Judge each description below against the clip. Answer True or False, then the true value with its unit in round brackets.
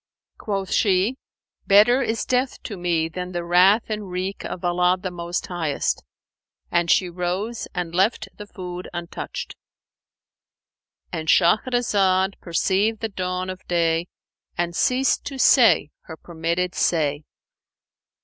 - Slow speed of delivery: True (125 wpm)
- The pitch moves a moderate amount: True (3.2 semitones)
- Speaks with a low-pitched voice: False (185 Hz)